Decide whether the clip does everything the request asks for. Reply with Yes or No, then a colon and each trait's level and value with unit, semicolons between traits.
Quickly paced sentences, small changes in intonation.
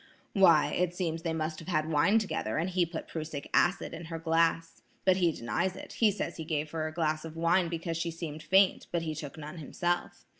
Yes: fast, 220 wpm; narrow, 2.0 semitones